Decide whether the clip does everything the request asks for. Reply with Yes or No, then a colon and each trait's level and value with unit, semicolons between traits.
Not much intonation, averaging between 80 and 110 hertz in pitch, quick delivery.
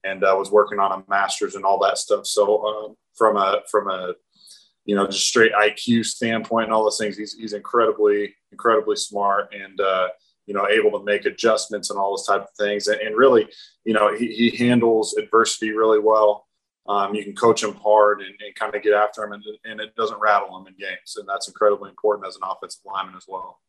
Yes: narrow, 2.0 semitones; low, 105 Hz; fast, 225 wpm